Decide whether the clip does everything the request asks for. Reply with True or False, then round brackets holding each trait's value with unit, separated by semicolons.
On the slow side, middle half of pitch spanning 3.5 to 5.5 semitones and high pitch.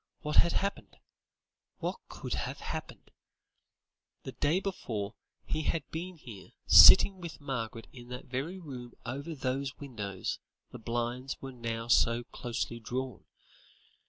False (130 wpm; 4.3 semitones; 130 Hz)